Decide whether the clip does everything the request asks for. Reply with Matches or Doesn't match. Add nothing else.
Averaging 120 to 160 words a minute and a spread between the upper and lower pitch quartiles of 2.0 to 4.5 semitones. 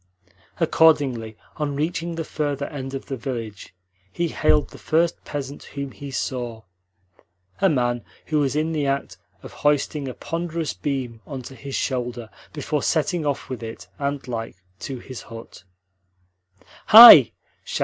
Matches